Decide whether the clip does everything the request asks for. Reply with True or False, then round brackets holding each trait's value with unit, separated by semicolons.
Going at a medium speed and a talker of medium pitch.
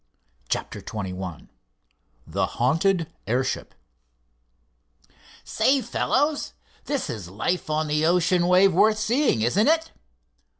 False (100 wpm; 175 Hz)